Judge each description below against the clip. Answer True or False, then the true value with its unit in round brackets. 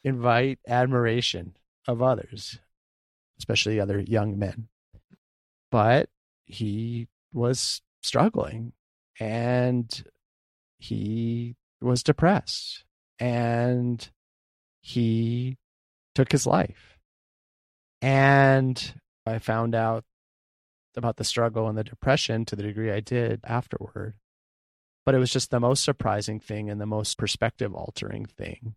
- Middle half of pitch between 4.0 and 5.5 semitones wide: False (3.3 semitones)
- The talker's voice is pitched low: True (115 Hz)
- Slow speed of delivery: True (105 wpm)